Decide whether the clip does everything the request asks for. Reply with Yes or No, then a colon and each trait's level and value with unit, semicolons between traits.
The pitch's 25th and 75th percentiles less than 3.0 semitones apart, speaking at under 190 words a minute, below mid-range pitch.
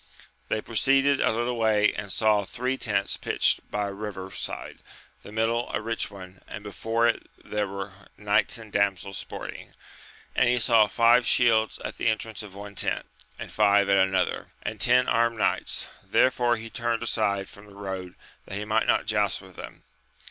Yes: narrow, 2.6 semitones; average, 180 wpm; low, 105 Hz